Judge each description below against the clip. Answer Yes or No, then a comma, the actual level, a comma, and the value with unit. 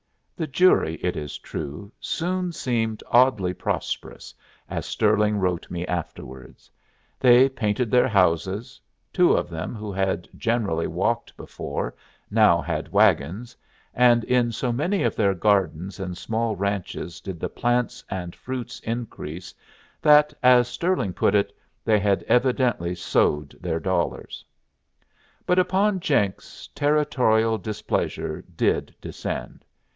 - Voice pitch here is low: Yes, low, 110 Hz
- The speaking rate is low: Yes, slow, 125 wpm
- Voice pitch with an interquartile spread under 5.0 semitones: No, wide, 5.4 semitones